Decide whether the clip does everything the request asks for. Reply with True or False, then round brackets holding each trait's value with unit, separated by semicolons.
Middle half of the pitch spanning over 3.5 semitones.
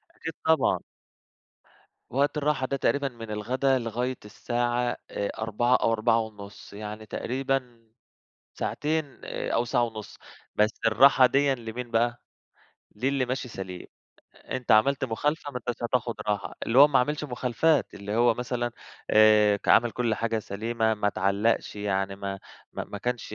False (3.2 semitones)